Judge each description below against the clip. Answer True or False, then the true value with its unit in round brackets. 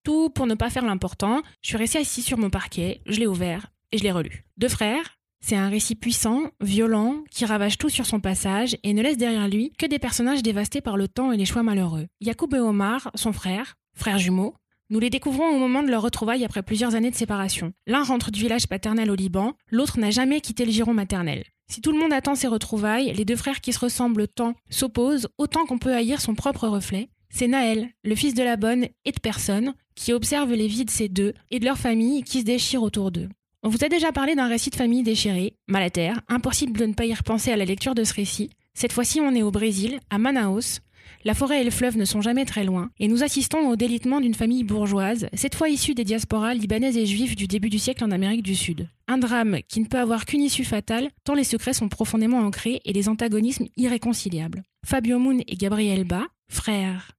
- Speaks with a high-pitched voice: True (230 Hz)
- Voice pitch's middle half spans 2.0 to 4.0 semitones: True (3.5 semitones)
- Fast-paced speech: True (235 wpm)